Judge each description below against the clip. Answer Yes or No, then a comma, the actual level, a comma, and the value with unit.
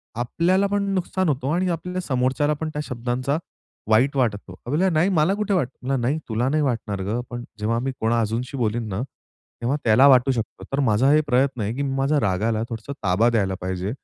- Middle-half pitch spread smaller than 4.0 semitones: No, average, 4.9 semitones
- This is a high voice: No, low, 130 Hz